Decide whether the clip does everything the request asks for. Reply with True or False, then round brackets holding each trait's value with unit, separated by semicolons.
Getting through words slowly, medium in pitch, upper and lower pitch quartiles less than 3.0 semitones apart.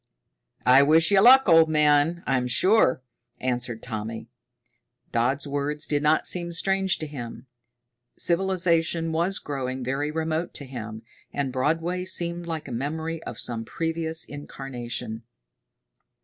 False (130 wpm; 150 Hz; 4.5 semitones)